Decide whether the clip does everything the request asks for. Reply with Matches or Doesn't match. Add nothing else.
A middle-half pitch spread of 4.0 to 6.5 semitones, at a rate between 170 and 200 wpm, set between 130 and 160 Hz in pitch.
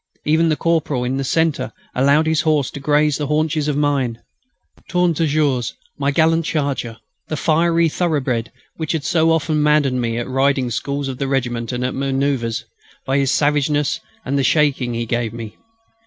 Doesn't match